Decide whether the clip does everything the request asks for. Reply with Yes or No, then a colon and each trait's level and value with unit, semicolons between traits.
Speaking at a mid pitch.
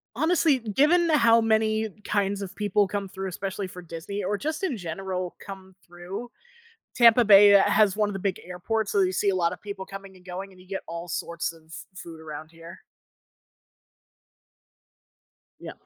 No: high, 195 Hz